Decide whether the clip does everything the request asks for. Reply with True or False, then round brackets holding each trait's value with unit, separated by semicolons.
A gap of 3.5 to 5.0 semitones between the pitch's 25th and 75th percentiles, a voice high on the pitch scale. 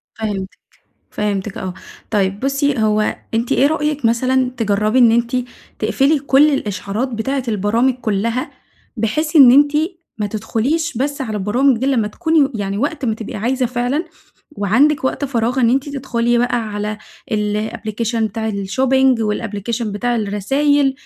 True (4.2 semitones; 235 Hz)